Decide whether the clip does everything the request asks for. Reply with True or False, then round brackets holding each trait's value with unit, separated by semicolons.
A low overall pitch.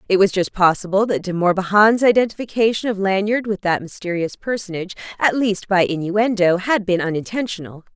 False (195 Hz)